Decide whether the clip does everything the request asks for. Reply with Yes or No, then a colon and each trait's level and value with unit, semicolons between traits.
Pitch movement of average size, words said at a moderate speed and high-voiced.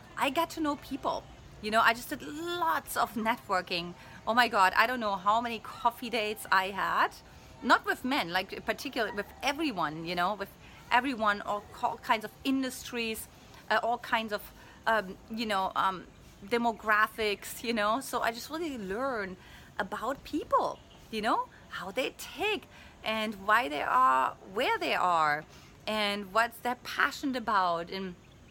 Yes: average, 4.3 semitones; average, 160 wpm; high, 225 Hz